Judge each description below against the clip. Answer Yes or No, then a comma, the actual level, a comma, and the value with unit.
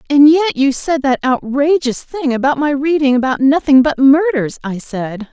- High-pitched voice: Yes, very high, 280 Hz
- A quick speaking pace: No, average, 180 wpm